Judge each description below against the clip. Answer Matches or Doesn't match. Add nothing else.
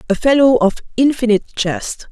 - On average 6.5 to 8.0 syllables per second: Doesn't match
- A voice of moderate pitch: Doesn't match